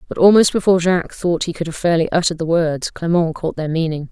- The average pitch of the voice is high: No, medium, 170 Hz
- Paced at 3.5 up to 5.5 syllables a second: No, 6.4 syllables/s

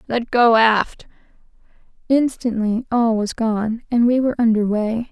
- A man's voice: No, female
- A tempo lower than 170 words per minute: Yes, average, 140 wpm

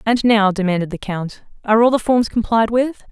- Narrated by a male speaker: No, female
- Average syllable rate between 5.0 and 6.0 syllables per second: Yes, 5.4 syllables/s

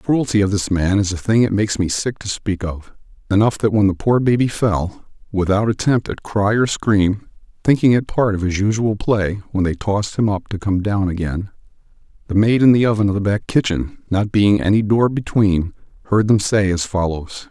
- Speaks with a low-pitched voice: Yes, low, 105 Hz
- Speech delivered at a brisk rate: Yes, fast, 215 wpm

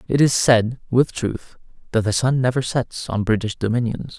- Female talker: No, male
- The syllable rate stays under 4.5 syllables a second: No, 4.8 syllables/s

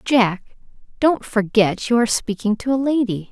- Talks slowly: No, average, 165 wpm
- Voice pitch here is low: No, high, 230 Hz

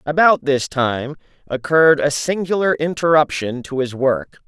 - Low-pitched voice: No, medium, 145 Hz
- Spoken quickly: No, slow, 135 wpm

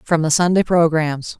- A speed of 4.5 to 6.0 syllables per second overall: Yes, 4.7 syllables/s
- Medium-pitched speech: Yes, medium, 160 Hz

